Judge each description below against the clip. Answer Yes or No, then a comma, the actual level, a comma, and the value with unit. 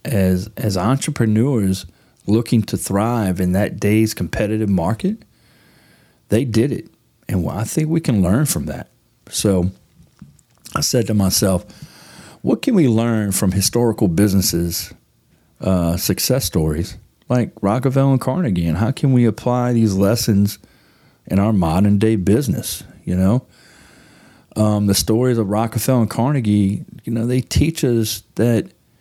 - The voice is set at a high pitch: No, low, 110 Hz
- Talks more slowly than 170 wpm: Yes, average, 145 wpm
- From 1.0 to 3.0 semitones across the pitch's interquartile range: No, average, 3.6 semitones